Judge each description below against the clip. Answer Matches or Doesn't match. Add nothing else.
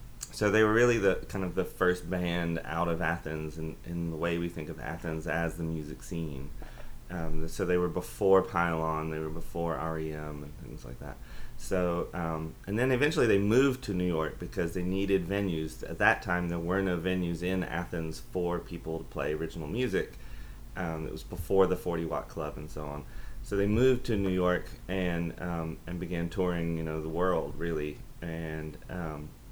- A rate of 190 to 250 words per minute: Matches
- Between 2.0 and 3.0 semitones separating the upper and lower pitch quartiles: Matches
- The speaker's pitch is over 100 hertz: Doesn't match